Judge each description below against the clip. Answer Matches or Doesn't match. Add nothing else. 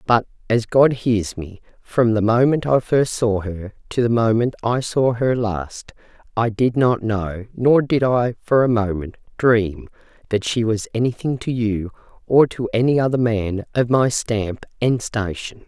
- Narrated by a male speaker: Doesn't match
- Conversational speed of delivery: Matches